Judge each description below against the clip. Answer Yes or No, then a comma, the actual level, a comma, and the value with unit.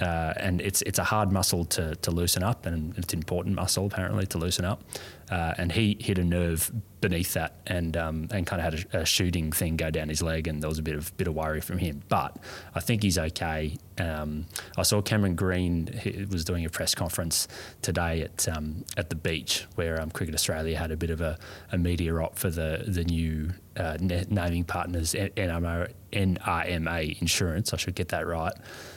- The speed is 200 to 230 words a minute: Yes, fast, 205 wpm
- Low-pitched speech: Yes, very low, 85 Hz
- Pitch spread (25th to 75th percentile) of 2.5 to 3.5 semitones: Yes, average, 2.9 semitones